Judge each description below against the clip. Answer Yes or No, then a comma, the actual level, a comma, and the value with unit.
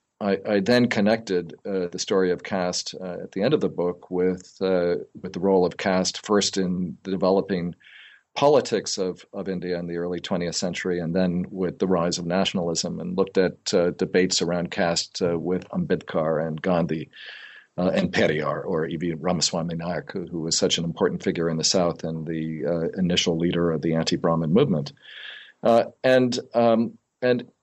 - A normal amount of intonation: No, narrow, 2.0 semitones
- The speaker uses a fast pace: No, average, 185 wpm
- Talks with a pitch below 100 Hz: Yes, very low, 90 Hz